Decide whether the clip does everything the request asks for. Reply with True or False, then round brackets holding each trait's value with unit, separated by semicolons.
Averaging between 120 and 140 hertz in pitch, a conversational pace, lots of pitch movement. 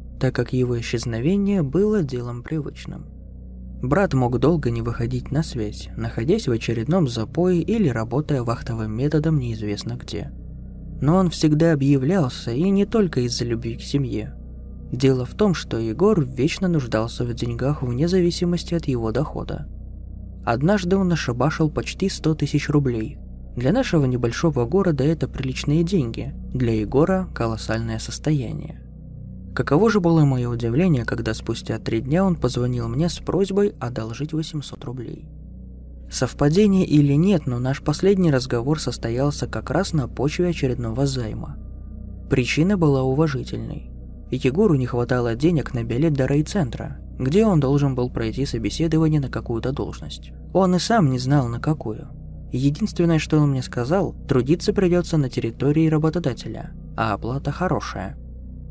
True (135 Hz; 140 wpm; 5.7 semitones)